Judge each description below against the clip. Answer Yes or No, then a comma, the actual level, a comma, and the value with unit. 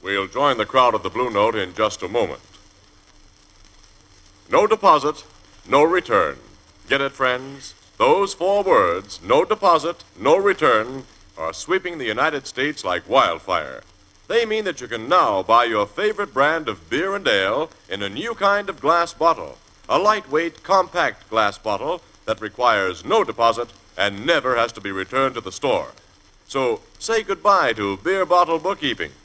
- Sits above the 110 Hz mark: Yes, medium, 140 Hz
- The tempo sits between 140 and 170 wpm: Yes, average, 160 wpm